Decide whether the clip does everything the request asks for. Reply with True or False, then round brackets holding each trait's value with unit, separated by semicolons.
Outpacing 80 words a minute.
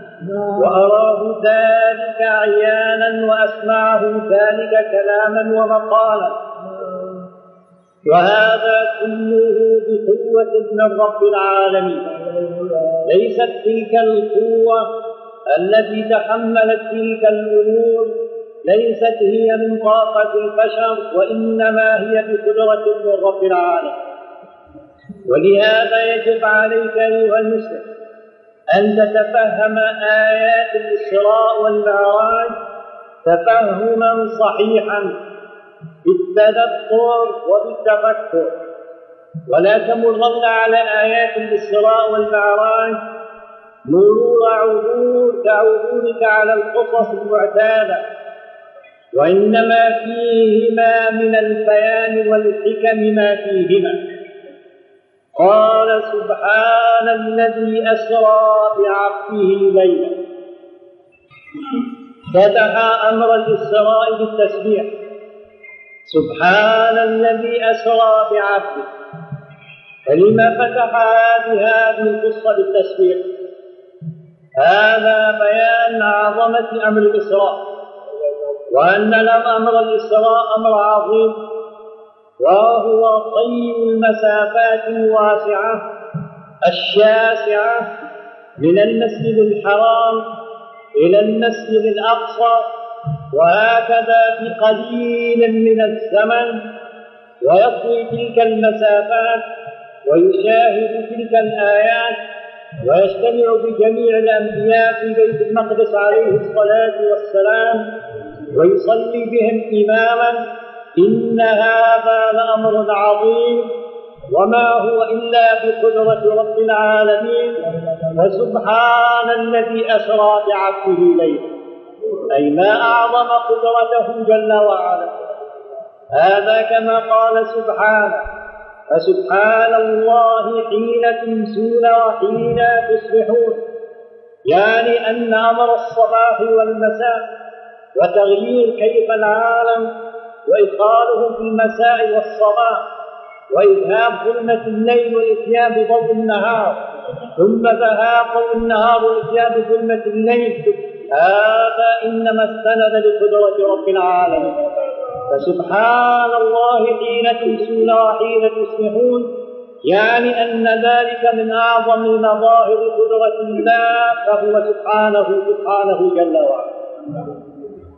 False (75 wpm)